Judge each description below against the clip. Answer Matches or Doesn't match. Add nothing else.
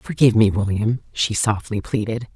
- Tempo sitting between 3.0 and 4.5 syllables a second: Doesn't match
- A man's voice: Doesn't match